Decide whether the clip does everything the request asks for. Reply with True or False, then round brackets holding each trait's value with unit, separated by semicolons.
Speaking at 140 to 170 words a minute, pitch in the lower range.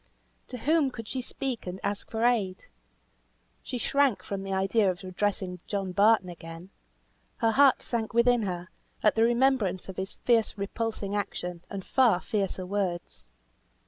False (155 wpm; 205 Hz)